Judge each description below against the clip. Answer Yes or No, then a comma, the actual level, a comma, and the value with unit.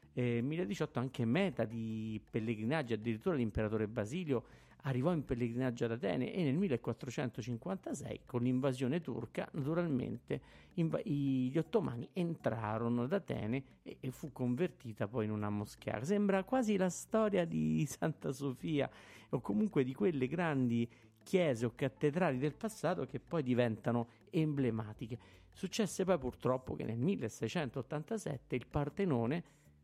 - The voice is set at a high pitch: No, low, 130 Hz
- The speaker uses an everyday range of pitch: No, wide, 5.9 semitones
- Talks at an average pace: Yes, average, 130 wpm